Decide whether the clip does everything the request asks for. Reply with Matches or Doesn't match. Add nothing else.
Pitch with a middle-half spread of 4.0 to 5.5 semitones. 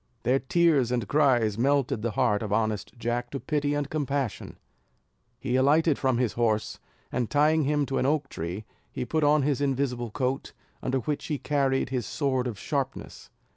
Doesn't match